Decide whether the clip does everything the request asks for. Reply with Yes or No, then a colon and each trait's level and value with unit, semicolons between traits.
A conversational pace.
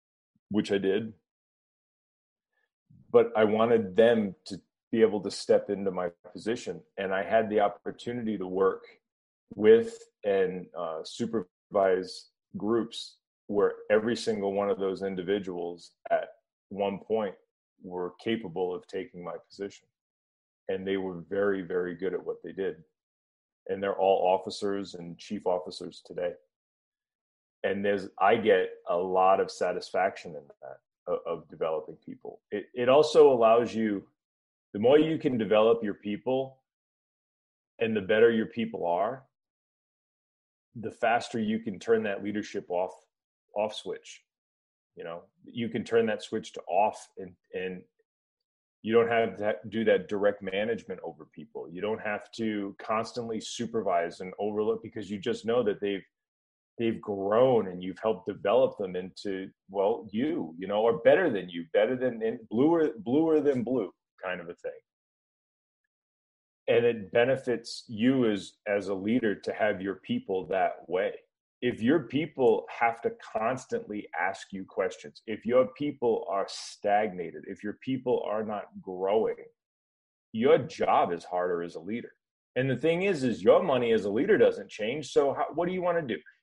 Yes: average, 155 wpm